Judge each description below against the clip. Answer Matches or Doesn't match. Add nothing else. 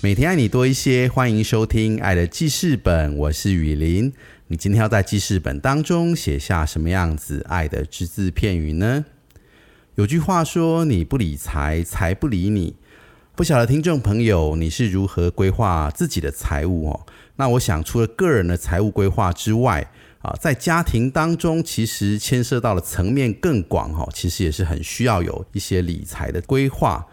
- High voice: Doesn't match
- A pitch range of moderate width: Doesn't match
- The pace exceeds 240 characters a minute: Matches